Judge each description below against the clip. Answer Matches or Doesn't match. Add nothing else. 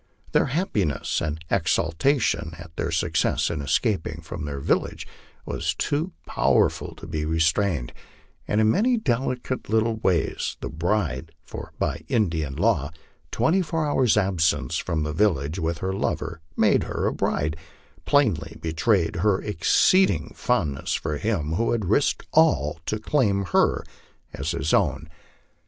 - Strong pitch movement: Matches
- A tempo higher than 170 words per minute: Doesn't match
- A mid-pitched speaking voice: Doesn't match